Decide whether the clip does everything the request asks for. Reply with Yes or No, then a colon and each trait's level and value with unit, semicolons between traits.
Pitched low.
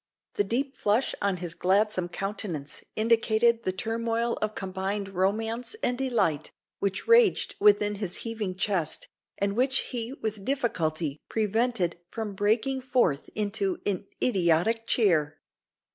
No: high, 210 Hz